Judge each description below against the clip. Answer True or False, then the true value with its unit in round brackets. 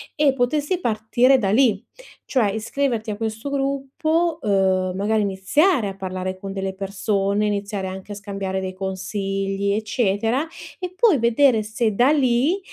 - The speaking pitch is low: False (215 Hz)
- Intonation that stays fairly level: False (5.4 semitones)